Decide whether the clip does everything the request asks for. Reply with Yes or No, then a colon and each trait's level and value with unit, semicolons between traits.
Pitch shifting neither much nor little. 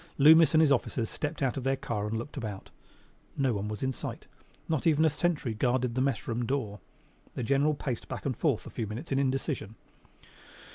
Yes: average, 4.1 semitones